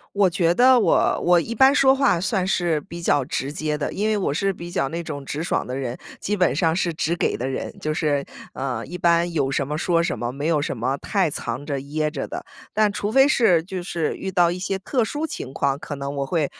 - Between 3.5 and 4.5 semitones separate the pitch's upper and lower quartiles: No, average, 5.1 semitones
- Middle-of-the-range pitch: Yes, medium, 170 Hz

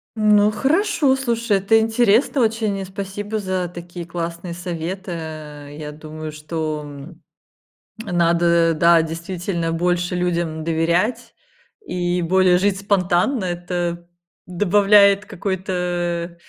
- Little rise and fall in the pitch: No, average, 3.1 semitones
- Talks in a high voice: No, medium, 175 Hz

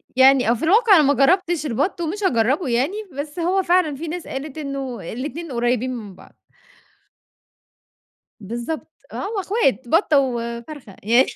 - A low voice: No, very high, 275 Hz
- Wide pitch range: Yes, wide, 5.7 semitones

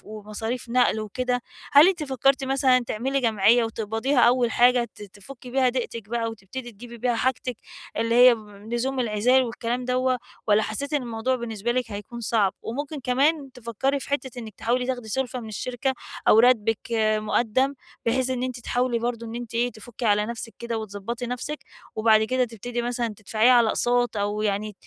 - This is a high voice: Yes, high, 240 Hz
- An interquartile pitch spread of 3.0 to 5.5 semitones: No, narrow, 2.4 semitones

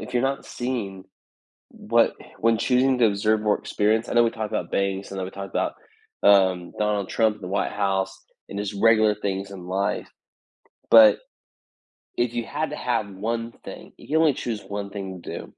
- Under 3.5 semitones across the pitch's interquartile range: Yes, average, 2.7 semitones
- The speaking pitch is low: Yes, low, 105 Hz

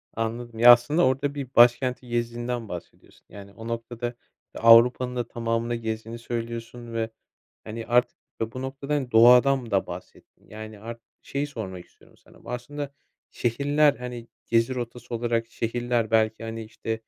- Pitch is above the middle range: No, low, 120 Hz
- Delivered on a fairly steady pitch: Yes, narrow, 1.6 semitones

